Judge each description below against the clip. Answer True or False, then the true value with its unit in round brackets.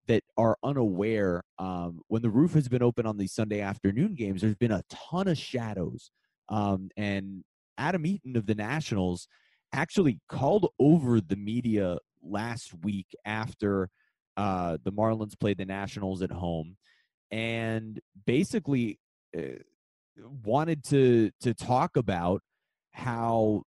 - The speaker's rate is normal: False (130 wpm)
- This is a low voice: True (110 Hz)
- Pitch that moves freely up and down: False (3.8 semitones)